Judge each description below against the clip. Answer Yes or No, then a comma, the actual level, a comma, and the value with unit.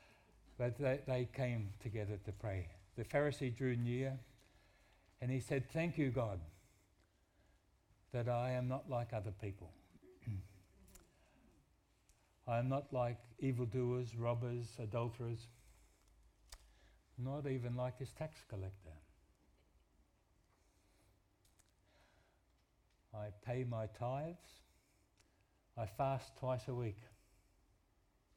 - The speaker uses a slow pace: Yes, slow, 95 wpm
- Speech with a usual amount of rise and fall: Yes, average, 4.5 semitones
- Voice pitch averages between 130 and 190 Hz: No, low, 110 Hz